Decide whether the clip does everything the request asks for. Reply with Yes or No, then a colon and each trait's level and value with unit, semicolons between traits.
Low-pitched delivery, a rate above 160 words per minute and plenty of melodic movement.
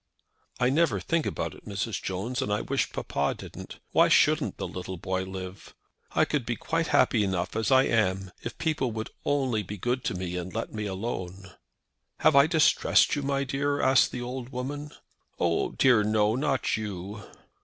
Yes: low, 115 Hz; average, 175 wpm; wide, 5.9 semitones